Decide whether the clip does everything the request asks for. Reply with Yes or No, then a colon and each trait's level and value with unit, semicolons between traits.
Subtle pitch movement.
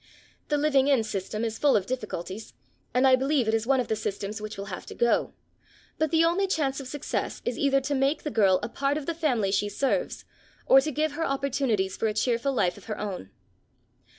No: average, 5.0 semitones